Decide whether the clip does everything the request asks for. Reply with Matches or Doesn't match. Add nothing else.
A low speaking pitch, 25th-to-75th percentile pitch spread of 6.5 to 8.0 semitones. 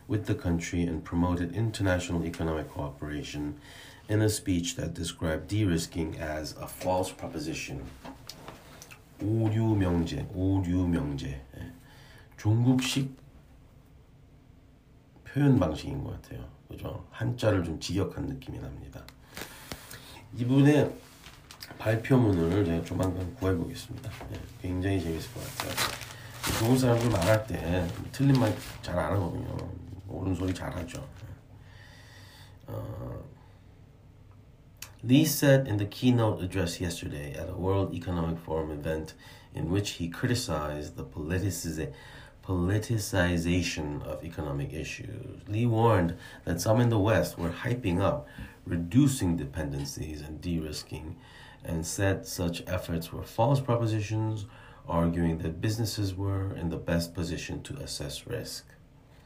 Doesn't match